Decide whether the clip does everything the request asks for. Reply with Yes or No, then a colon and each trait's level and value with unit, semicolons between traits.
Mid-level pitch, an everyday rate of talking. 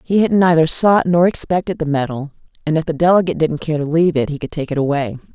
No: medium, 160 Hz; fast, 245 wpm